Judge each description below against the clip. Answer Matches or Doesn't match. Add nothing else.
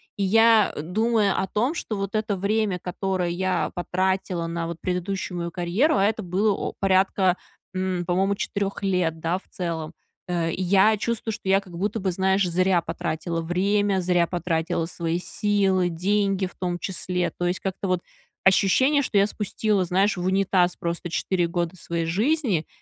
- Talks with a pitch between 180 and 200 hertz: Matches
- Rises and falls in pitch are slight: Matches